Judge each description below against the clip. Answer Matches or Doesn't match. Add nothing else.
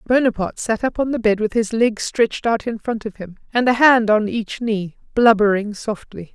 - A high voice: Matches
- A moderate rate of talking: Doesn't match